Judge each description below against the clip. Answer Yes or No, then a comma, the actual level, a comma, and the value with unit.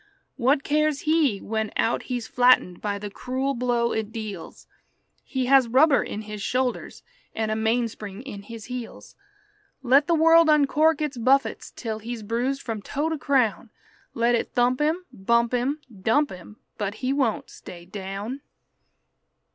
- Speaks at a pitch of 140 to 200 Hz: No, high, 245 Hz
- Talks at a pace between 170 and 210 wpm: No, average, 155 wpm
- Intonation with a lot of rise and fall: No, average, 4.1 semitones